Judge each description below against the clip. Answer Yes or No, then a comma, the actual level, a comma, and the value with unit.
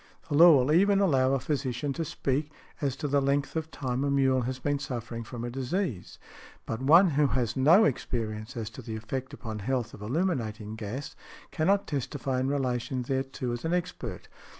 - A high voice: No, low, 130 Hz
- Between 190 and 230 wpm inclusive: Yes, average, 195 wpm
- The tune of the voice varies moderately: Yes, average, 3.4 semitones